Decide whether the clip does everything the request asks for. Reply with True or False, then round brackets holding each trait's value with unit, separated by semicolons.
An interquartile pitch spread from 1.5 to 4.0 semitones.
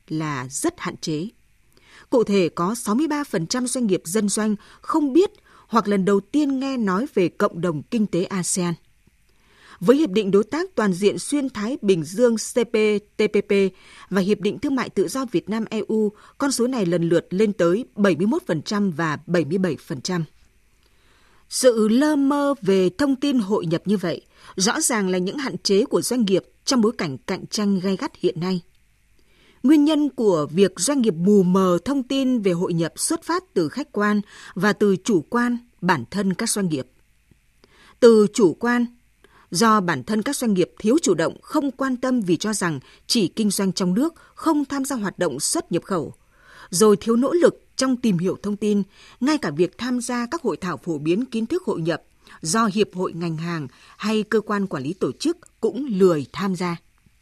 False (5.4 semitones)